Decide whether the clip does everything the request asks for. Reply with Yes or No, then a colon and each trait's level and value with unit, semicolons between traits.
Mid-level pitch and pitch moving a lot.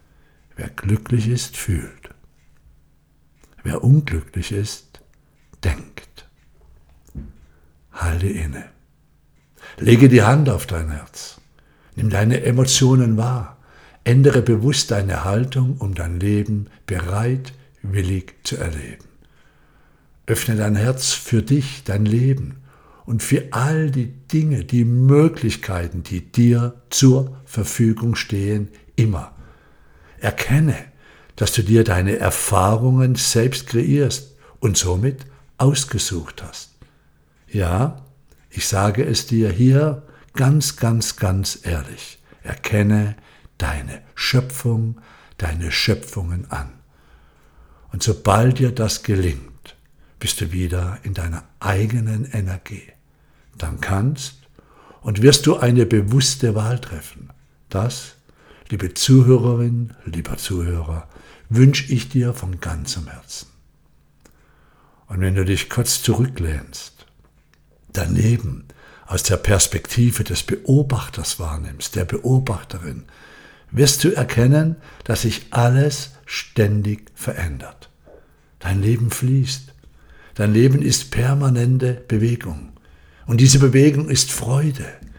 No: low, 110 Hz; wide, 6.2 semitones